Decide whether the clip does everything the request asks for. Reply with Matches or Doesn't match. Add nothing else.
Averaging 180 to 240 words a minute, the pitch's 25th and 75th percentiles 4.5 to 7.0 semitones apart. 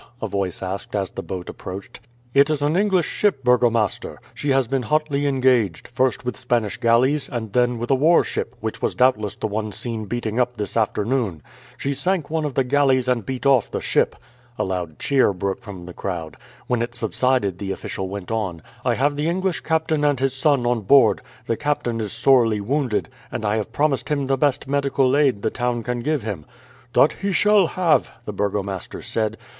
Matches